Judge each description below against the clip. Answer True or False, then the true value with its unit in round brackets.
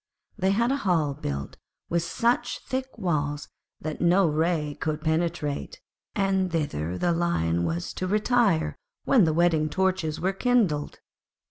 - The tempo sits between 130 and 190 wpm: True (140 wpm)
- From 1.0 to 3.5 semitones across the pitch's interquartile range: False (4.2 semitones)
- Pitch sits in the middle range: True (170 Hz)